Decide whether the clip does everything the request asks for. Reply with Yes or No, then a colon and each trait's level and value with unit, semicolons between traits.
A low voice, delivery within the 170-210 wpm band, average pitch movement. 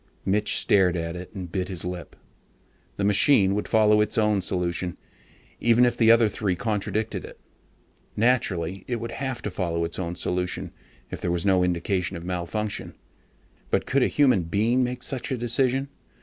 Yes: low, 100 Hz; average, 175 wpm; average, 4.5 semitones